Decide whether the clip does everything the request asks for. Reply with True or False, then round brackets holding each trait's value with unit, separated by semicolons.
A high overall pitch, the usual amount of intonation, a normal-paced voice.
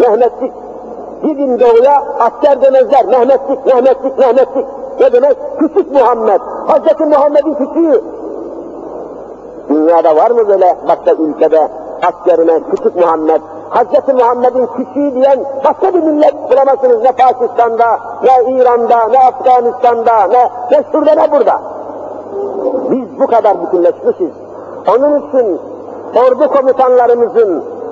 True (260 Hz; 4.3 semitones; 110 wpm)